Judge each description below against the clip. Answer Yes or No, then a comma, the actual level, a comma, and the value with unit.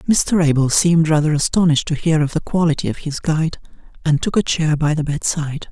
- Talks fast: Yes, fast, 210 wpm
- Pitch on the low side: No, medium, 155 Hz